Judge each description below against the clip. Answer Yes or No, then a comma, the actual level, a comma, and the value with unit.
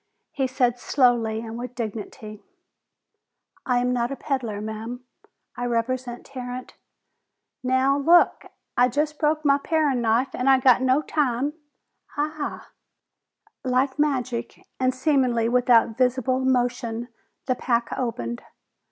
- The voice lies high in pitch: Yes, very high, 250 Hz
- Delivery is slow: Yes, slow, 130 wpm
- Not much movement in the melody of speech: Yes, narrow, 2.3 semitones